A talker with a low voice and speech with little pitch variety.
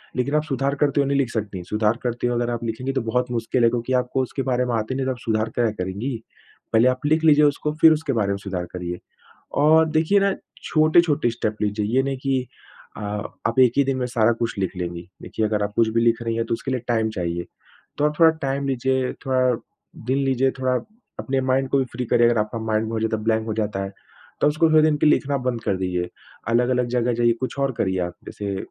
No: low, 120 Hz; average, 3.5 semitones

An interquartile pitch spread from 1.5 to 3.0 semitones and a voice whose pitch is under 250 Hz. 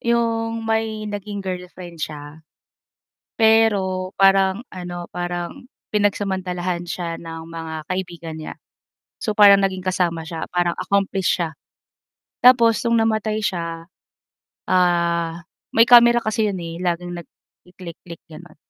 No: average, 3.7 semitones; medium, 185 Hz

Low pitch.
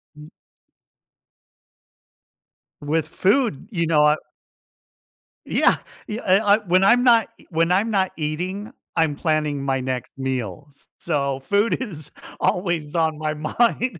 No: medium, 160 Hz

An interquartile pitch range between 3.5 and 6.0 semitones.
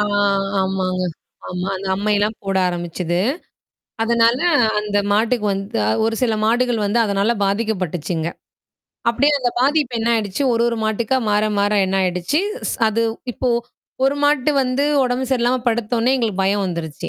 Yes: average, 4.0 semitones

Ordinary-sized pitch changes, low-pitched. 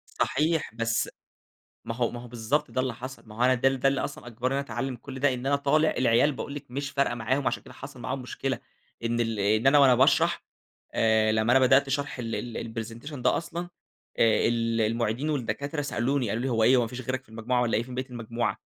Yes: average, 3.0 semitones; low, 125 Hz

